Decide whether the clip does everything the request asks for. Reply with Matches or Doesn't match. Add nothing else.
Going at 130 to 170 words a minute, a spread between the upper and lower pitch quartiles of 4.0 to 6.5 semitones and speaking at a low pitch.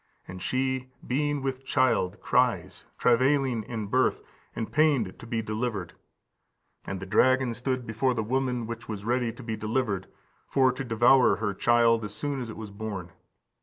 Doesn't match